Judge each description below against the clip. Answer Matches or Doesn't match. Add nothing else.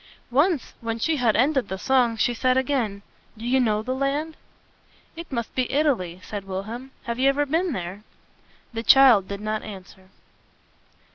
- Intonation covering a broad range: Doesn't match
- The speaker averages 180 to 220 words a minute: Doesn't match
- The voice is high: Matches